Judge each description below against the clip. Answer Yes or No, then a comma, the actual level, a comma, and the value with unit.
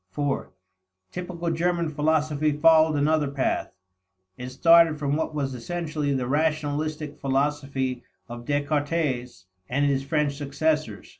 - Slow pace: Yes, slow, 120 wpm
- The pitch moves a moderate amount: No, narrow, 2.2 semitones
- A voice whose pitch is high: No, medium, 150 Hz